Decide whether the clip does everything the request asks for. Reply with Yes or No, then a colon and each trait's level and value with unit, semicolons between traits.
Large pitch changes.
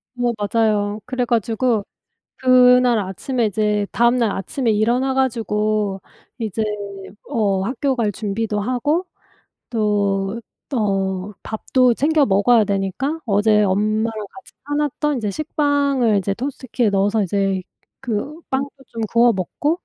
No: average, 3.9 semitones